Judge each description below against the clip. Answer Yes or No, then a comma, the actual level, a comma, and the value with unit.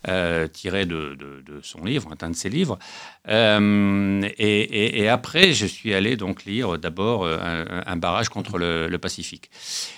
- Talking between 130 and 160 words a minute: No, average, 175 wpm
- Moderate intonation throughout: Yes, average, 3.8 semitones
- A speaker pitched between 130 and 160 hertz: No, very low, 95 Hz